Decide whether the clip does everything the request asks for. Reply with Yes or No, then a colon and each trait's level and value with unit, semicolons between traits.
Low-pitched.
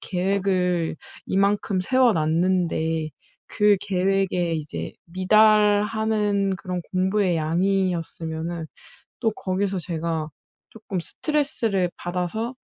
No: medium, 185 Hz